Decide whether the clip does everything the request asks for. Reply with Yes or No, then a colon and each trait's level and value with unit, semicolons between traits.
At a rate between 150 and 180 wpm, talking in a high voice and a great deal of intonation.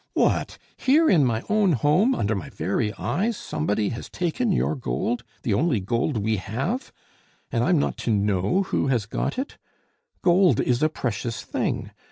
No: average, 170 wpm; low, 130 Hz; wide, 8.9 semitones